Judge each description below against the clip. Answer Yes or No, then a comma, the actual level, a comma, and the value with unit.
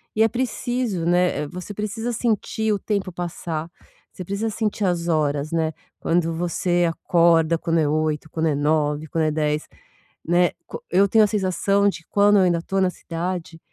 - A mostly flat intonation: No, average, 3.8 semitones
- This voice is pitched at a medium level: Yes, medium, 175 Hz